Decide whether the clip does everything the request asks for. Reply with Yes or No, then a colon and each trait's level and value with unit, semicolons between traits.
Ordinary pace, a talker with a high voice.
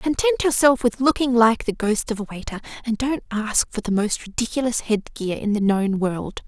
No: fast, 215 wpm; high, 220 Hz